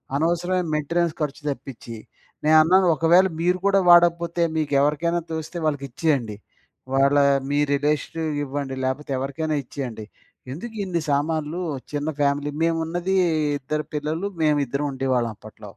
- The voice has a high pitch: No, medium, 150 Hz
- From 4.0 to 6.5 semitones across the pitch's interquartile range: No, average, 3.3 semitones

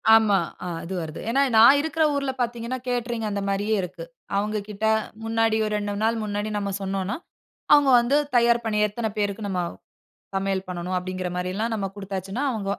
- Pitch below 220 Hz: Yes, high, 210 Hz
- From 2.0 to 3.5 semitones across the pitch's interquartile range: Yes, average, 3.1 semitones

